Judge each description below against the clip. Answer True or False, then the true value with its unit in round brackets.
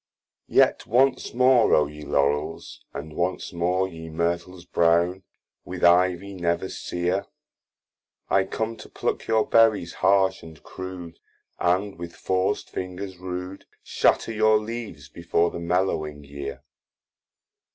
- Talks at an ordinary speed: False (125 wpm)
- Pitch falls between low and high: False (90 Hz)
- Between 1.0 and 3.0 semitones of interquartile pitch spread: True (2.5 semitones)